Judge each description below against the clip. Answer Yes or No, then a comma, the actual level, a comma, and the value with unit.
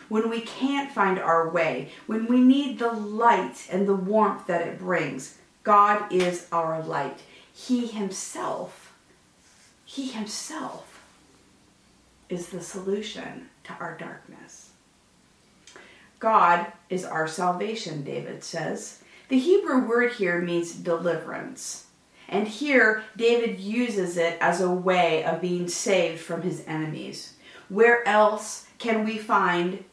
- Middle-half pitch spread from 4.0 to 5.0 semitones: Yes, average, 4.5 semitones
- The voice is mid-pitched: No, high, 195 Hz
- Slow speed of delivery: Yes, slow, 125 wpm